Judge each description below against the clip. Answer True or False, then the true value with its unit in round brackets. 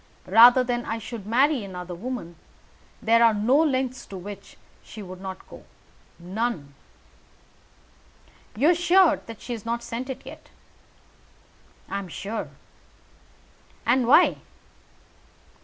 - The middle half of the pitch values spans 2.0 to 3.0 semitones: False (4.4 semitones)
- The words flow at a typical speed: False (125 wpm)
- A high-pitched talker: True (230 Hz)